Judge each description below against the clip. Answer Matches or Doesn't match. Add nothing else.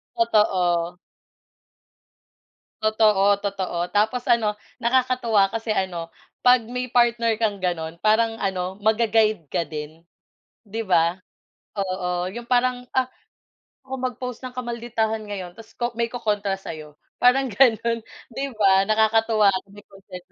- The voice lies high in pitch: Matches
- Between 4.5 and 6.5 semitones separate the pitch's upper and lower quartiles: Doesn't match